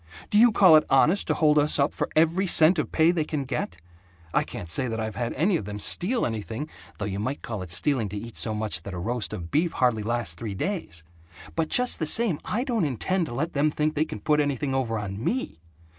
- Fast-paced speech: Yes, fast, 245 wpm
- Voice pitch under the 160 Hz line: Yes, medium, 140 Hz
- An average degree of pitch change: No, wide, 6.9 semitones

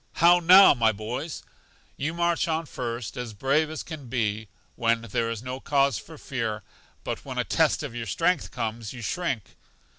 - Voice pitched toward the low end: Yes, low, 125 Hz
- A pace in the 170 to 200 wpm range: Yes, average, 180 wpm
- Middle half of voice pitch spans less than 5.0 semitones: No, wide, 5.5 semitones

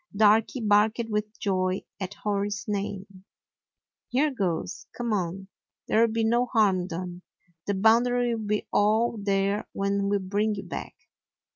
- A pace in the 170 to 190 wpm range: No, average, 145 wpm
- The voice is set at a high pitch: Yes, high, 205 Hz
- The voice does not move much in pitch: Yes, narrow, 2.1 semitones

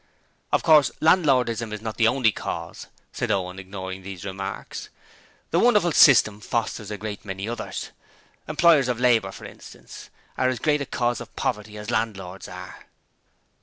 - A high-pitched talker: No, low, 115 Hz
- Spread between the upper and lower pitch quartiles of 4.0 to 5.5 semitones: Yes, average, 4.5 semitones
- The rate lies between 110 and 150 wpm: No, average, 160 wpm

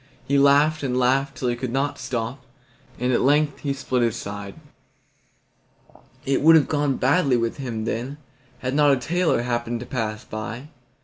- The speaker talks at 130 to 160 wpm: No, average, 175 wpm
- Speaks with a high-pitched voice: No, low, 130 Hz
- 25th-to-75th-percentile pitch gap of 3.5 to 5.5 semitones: No, average, 3.1 semitones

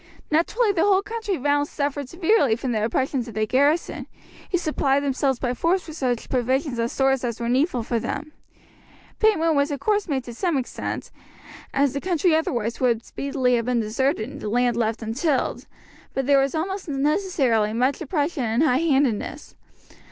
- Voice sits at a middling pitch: No, very high, 275 Hz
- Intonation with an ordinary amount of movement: Yes, average, 4.6 semitones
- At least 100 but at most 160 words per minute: No, average, 180 wpm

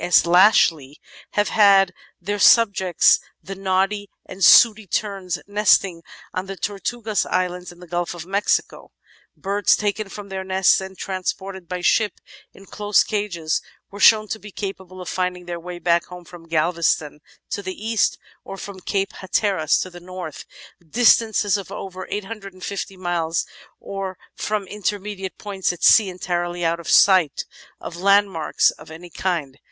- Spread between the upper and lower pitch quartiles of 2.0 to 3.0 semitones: Yes, narrow, 2.5 semitones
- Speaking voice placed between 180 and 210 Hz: Yes, high, 190 Hz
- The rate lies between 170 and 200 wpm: No, average, 160 wpm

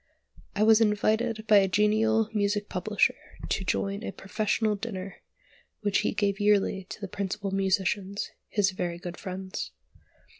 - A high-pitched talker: Yes, high, 200 Hz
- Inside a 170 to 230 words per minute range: No, average, 145 wpm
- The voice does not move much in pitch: Yes, narrow, 1.9 semitones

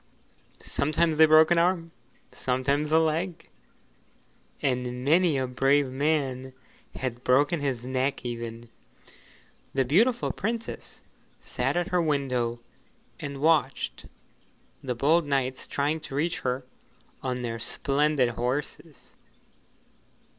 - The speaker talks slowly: Yes, slow, 110 wpm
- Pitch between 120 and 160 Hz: Yes, medium, 140 Hz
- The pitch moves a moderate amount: Yes, average, 3.8 semitones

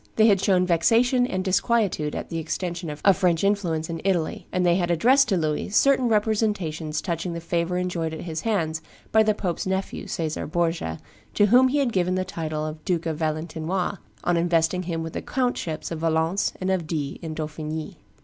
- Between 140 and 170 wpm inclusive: No, average, 195 wpm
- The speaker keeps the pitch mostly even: No, average, 3.5 semitones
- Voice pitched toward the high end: No, medium, 175 Hz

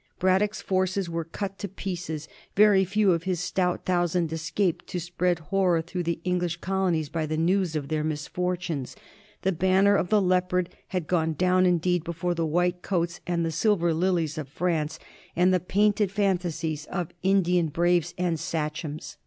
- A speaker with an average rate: Yes, average, 175 wpm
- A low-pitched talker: No, medium, 175 Hz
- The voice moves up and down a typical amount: No, narrow, 2.2 semitones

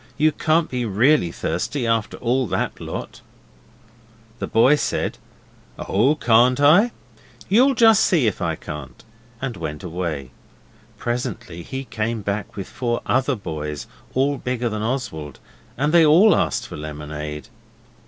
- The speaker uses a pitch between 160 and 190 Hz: No, low, 120 Hz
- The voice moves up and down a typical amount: No, wide, 8.7 semitones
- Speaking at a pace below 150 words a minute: Yes, average, 140 wpm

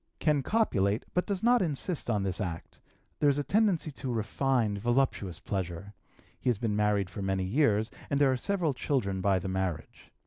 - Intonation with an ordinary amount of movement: No, wide, 6.8 semitones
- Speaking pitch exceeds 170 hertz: No, low, 110 Hz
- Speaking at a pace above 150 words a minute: Yes, average, 185 wpm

